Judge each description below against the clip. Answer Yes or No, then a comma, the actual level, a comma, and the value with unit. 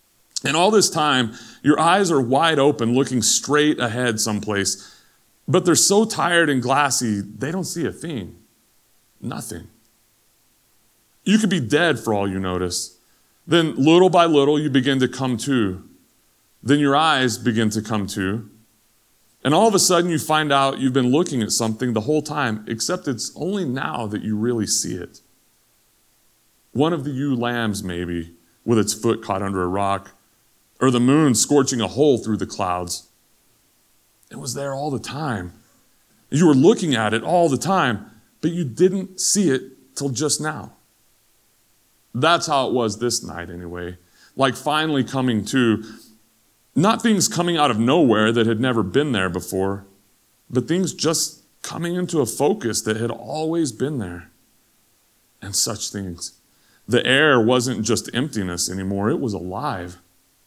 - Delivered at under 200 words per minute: Yes, average, 165 wpm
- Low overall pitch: Yes, low, 120 Hz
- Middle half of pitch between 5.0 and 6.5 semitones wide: Yes, wide, 5.6 semitones